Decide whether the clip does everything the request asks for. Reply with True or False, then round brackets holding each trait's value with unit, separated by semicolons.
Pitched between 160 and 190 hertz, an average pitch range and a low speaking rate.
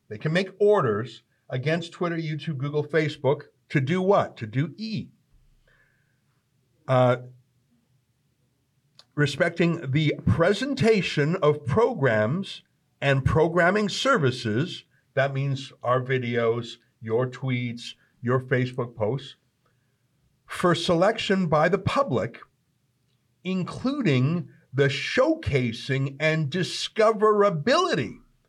False (140 Hz; 4.3 semitones; 90 wpm)